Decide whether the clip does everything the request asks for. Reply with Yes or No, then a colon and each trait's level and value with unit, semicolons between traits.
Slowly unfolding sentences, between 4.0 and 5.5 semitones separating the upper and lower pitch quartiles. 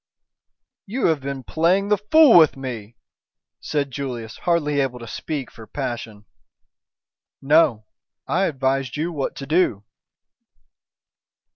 Yes: slow, 120 wpm; average, 5.1 semitones